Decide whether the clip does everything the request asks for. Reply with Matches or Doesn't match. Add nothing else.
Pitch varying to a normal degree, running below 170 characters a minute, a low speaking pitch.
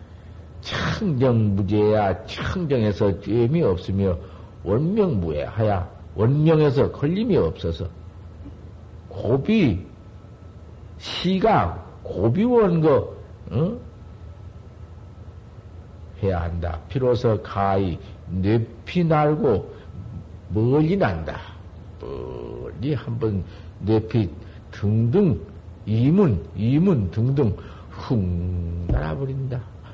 Matches